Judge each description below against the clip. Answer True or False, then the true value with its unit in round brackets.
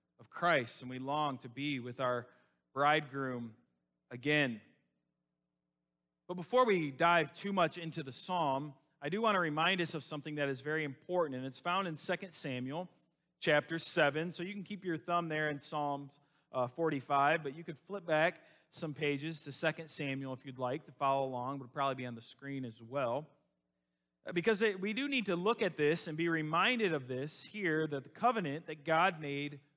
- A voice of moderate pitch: True (150 Hz)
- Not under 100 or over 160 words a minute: False (190 wpm)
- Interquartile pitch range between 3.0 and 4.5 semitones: True (4.1 semitones)